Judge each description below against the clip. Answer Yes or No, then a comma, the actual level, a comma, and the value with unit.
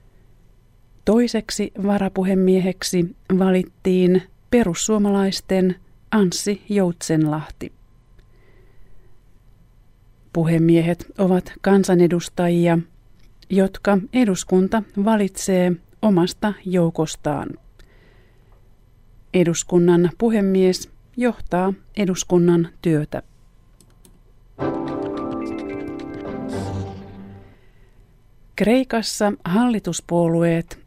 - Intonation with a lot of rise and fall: Yes, wide, 8.0 semitones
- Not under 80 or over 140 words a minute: No, slow, 40 wpm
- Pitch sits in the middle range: Yes, medium, 175 Hz